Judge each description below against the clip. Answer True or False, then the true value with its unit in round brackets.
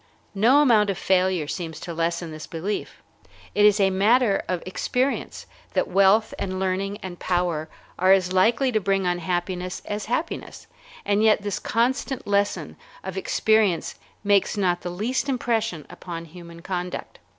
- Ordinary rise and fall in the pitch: True (3.2 semitones)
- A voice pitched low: False (195 Hz)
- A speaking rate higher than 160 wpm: False (150 wpm)